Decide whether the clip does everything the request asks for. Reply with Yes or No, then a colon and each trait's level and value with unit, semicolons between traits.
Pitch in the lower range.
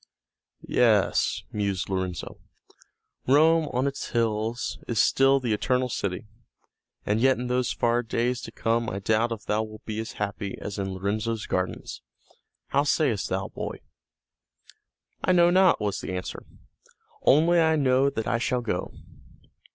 Yes: low, 115 Hz